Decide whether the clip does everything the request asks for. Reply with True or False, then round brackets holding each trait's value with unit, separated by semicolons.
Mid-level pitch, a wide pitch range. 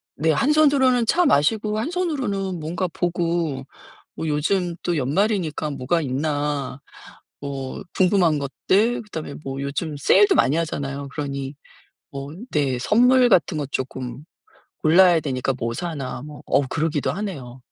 True (155 Hz; 5.7 semitones)